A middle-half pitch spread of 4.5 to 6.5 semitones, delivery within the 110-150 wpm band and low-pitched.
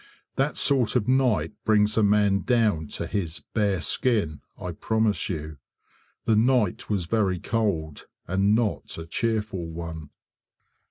Yes: average, 4.9 semitones; average, 140 wpm; low, 105 Hz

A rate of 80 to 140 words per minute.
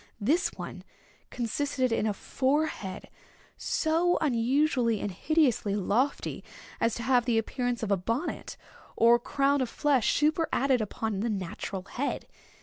Yes: slow, 135 wpm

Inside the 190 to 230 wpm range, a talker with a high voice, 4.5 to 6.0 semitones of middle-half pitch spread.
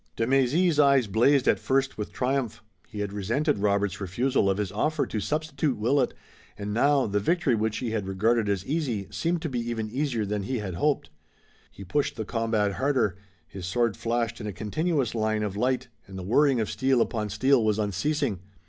No: average, 195 wpm; low, 115 Hz; average, 4.9 semitones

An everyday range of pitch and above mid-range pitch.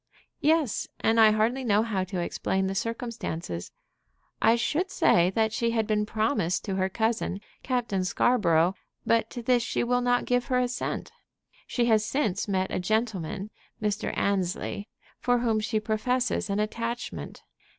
Yes: average, 3.6 semitones; high, 220 Hz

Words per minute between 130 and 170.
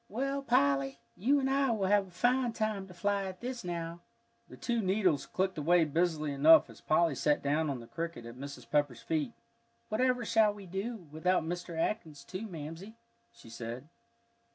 No: average, 180 wpm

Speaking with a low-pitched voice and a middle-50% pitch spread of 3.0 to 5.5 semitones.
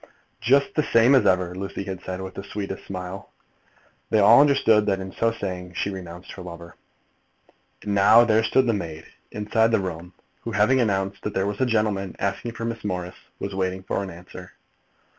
Yes: low, 100 Hz; average, 3.3 semitones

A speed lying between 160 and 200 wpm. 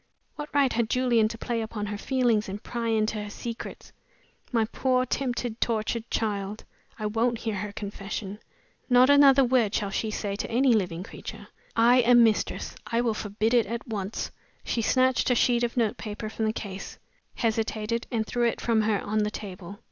Yes: average, 185 wpm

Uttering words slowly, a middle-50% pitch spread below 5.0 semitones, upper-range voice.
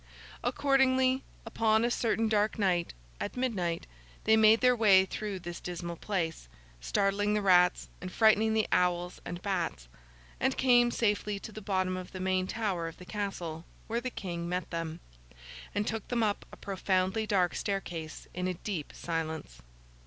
No: average, 165 wpm; average, 3.8 semitones; high, 195 Hz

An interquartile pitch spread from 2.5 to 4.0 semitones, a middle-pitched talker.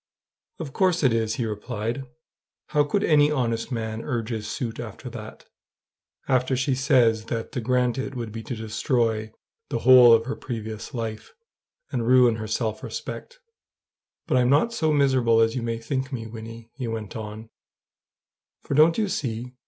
No: average, 2.8 semitones; low, 120 Hz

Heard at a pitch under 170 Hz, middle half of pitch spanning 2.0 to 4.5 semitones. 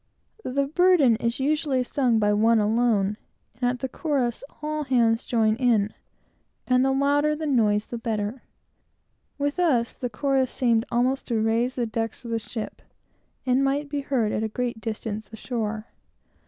No: high, 245 Hz; average, 3.4 semitones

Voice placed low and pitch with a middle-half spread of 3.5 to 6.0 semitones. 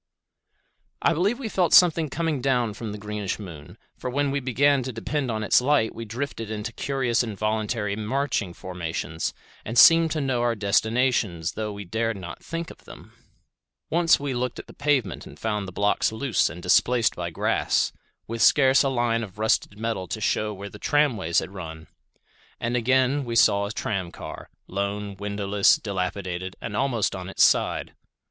Yes: low, 110 Hz; average, 4.7 semitones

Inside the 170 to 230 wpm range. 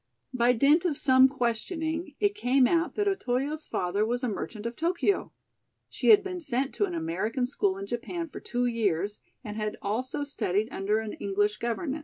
Yes: average, 185 wpm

